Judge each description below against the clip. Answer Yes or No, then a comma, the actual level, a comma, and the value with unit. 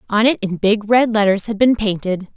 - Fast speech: Yes, fast, 230 wpm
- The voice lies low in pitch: No, high, 210 Hz